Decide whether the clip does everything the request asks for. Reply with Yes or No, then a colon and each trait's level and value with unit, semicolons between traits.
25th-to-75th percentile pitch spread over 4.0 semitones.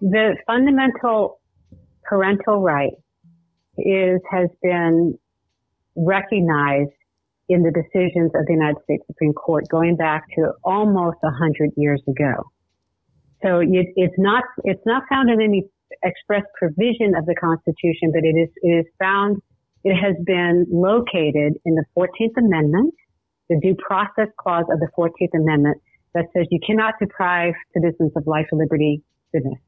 No: average, 3.4 semitones